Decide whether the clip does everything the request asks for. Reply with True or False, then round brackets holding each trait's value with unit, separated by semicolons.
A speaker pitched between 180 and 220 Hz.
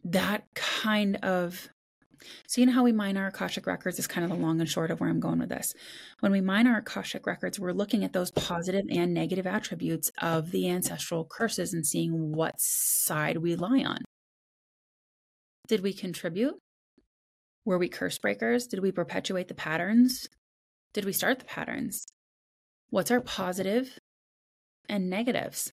True (190 Hz)